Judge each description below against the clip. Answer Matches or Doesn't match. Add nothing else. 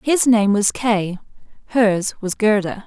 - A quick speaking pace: Doesn't match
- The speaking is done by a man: Doesn't match